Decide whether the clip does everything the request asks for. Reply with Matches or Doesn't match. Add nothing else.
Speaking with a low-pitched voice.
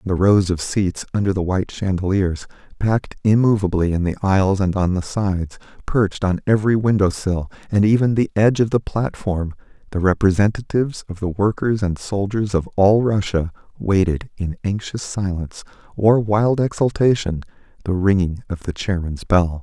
Matches